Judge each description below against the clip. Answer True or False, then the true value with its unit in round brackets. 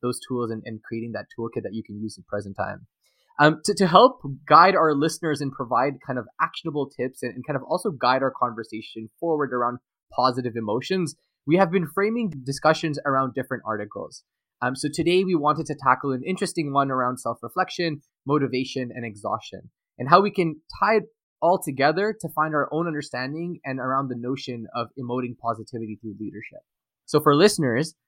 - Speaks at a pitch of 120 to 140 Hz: True (135 Hz)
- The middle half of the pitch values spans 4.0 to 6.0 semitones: True (4.6 semitones)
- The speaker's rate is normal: True (185 wpm)